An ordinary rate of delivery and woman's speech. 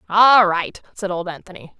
Yes: average, 165 wpm; female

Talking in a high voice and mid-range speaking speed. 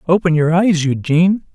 No: medium, 170 Hz; average, 155 wpm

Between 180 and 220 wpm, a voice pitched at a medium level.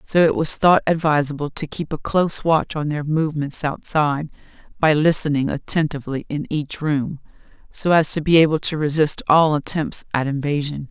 No: average, 170 wpm; medium, 150 Hz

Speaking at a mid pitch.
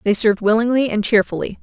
No: high, 220 Hz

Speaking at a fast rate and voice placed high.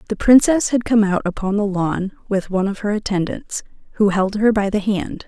Yes: fast, 215 wpm; high, 205 Hz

